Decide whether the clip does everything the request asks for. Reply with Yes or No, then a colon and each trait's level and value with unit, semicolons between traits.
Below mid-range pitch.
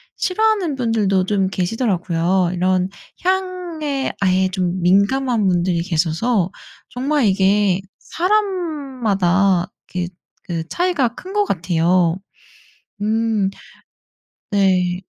No: high, 195 Hz